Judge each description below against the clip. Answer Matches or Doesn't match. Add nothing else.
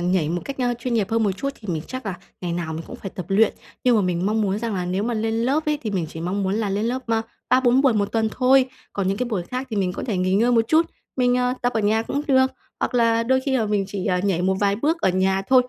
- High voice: Matches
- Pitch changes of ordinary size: Matches